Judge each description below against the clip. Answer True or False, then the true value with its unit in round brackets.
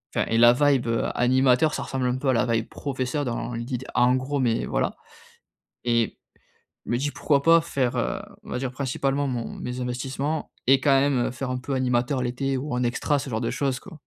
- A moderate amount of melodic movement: False (2.2 semitones)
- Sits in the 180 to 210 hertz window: False (130 Hz)